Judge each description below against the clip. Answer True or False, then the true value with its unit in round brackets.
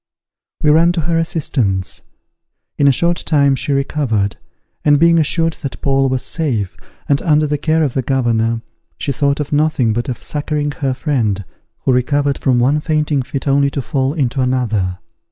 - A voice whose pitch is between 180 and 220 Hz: False (140 Hz)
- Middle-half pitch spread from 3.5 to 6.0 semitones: False (3.1 semitones)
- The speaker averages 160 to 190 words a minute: True (175 wpm)